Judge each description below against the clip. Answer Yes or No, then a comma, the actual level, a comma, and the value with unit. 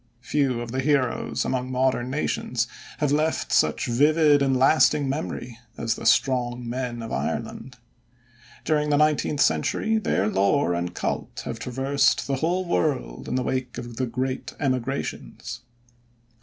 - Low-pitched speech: Yes, low, 130 Hz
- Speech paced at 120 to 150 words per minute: Yes, average, 145 wpm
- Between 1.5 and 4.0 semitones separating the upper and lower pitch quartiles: Yes, average, 3.1 semitones